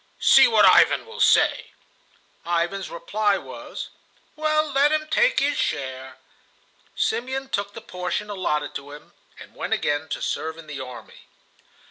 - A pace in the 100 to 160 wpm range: Yes, average, 145 wpm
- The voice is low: No, high, 195 Hz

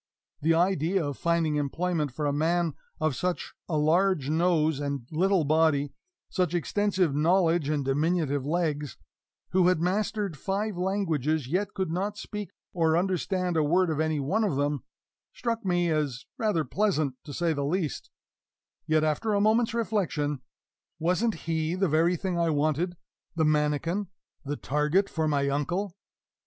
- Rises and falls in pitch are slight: No, average, 3.8 semitones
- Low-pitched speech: No, medium, 165 Hz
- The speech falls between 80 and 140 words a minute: No, average, 155 wpm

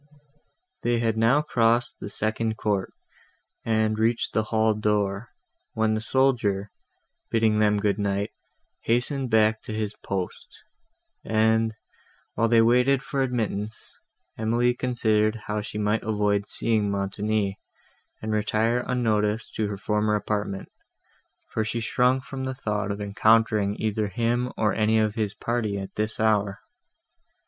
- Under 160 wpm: Yes, average, 140 wpm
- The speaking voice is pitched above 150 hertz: No, low, 110 Hz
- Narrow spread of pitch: Yes, narrow, 1.7 semitones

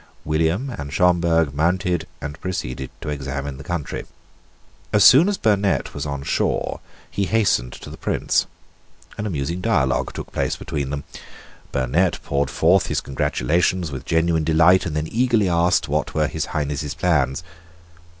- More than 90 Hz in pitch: No, very low, 80 Hz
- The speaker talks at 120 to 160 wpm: Yes, average, 150 wpm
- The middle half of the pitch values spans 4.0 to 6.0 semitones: Yes, average, 4.3 semitones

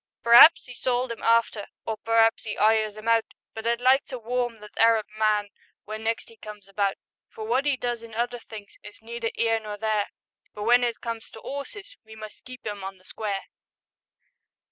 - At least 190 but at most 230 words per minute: Yes, average, 200 wpm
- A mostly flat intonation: Yes, narrow, 1.9 semitones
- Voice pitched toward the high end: Yes, high, 225 Hz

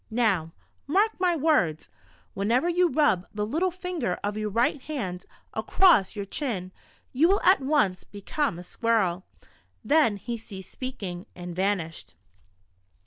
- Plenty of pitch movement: Yes, wide, 8.3 semitones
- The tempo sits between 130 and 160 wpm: Yes, average, 140 wpm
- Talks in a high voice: Yes, high, 220 Hz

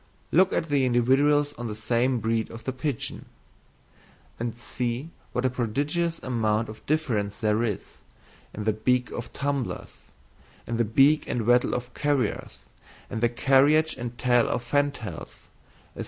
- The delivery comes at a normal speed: Yes, average, 155 wpm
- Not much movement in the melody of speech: No, average, 3.7 semitones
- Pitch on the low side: Yes, low, 125 Hz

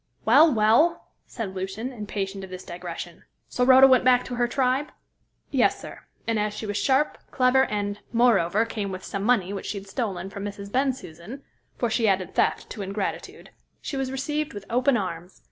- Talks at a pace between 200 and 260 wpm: No, average, 185 wpm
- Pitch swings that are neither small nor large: Yes, average, 4.7 semitones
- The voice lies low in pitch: No, high, 215 Hz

